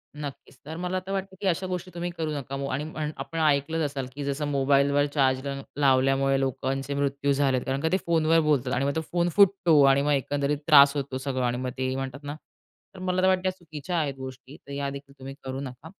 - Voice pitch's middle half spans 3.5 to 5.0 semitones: No, average, 3.0 semitones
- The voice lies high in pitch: No, medium, 140 Hz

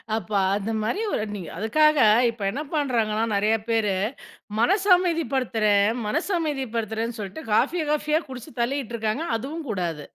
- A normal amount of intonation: No, wide, 6.0 semitones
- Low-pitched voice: No, high, 230 Hz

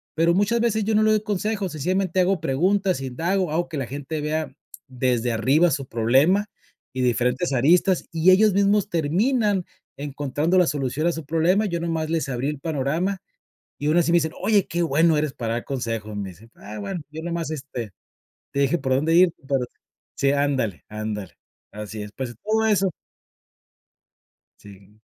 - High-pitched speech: No, medium, 155 Hz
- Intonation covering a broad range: Yes, wide, 5.9 semitones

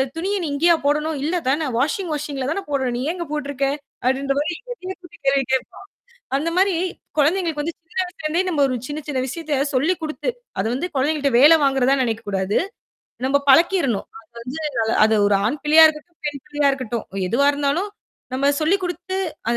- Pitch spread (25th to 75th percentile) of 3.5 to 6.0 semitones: Yes, average, 3.9 semitones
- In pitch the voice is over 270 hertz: Yes, very high, 295 Hz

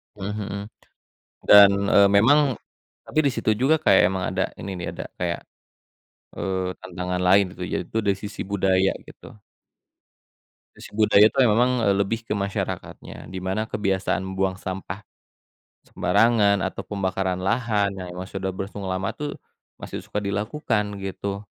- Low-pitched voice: Yes, low, 100 Hz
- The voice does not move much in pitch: Yes, narrow, 1.9 semitones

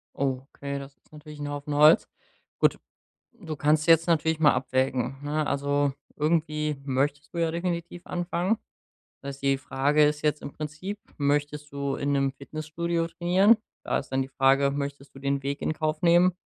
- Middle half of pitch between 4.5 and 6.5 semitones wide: No, narrow, 2.6 semitones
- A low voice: No, medium, 150 Hz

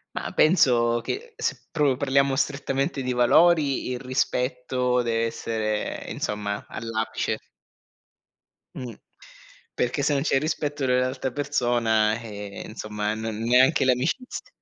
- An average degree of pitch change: Yes, average, 3.4 semitones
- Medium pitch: No, low, 125 Hz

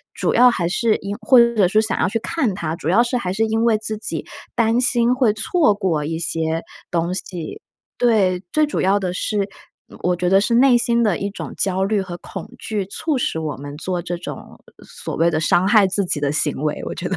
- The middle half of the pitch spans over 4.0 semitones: Yes, average, 5.0 semitones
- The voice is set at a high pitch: Yes, high, 200 Hz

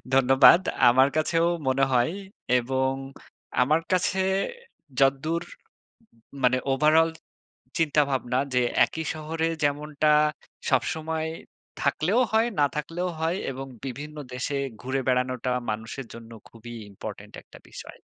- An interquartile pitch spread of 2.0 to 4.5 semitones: Yes, average, 4.0 semitones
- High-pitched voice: No, medium, 140 Hz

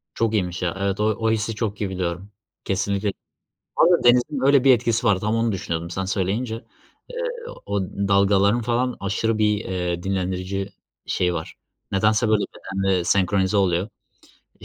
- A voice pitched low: Yes, low, 100 Hz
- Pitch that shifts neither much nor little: Yes, average, 3.1 semitones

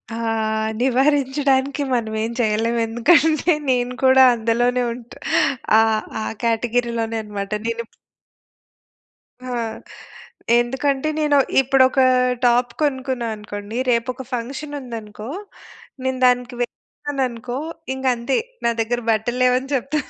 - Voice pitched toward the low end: No, high, 245 Hz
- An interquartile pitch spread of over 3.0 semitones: No, narrow, 2.6 semitones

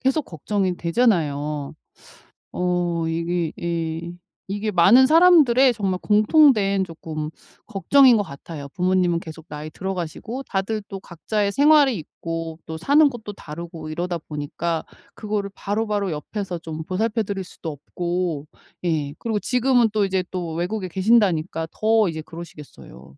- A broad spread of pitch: No, average, 4.8 semitones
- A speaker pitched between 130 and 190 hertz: Yes, medium, 185 Hz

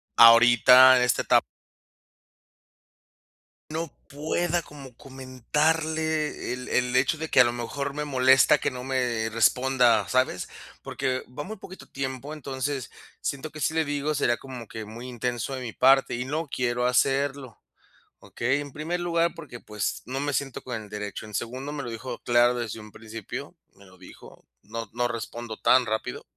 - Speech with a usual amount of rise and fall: Yes, average, 3.2 semitones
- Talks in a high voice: No, low, 130 Hz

